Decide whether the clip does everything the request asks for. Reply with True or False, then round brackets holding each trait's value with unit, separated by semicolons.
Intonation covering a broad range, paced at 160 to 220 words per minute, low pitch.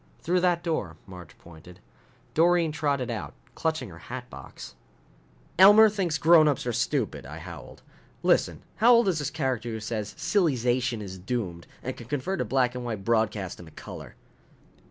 True (7.3 semitones; 165 wpm; 125 Hz)